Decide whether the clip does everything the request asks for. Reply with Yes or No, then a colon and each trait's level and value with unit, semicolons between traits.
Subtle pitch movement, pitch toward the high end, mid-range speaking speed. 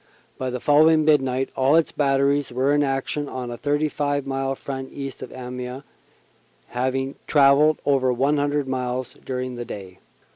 No: narrow, 2.1 semitones; low, 135 Hz; average, 150 wpm